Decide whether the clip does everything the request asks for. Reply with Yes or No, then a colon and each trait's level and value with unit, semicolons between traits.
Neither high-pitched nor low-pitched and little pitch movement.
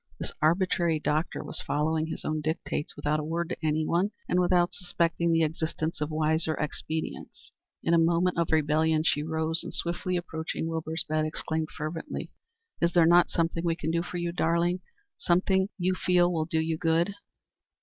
Yes: medium, 165 Hz; narrow, 1.6 semitones